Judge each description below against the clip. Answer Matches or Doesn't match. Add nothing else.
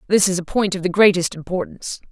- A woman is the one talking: Matches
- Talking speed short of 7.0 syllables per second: Matches